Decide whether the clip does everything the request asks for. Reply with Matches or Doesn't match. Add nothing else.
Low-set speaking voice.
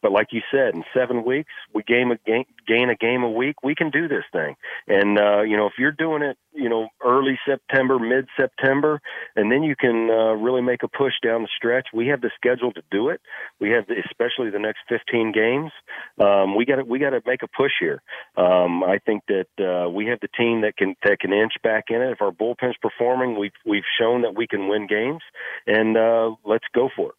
Matches